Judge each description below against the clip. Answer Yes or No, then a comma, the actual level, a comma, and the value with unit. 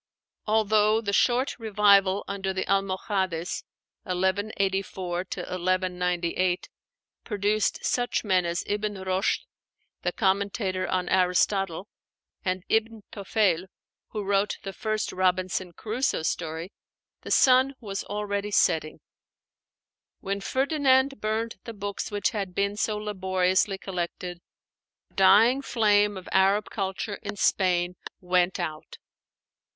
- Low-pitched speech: No, high, 195 Hz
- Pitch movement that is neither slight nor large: No, narrow, 2.3 semitones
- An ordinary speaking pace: No, slow, 110 wpm